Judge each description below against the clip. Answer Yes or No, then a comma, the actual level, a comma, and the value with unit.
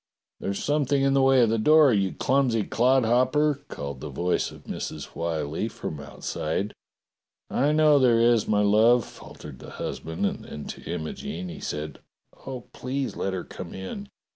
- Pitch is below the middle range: Yes, low, 115 Hz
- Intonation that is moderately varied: No, wide, 7.6 semitones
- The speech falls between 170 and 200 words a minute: Yes, average, 175 wpm